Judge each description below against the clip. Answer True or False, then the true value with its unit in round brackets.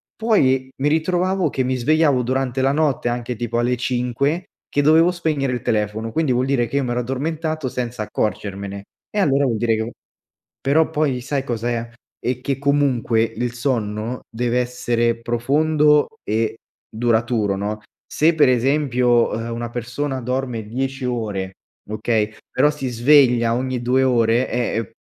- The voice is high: False (125 Hz)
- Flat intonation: False (3.2 semitones)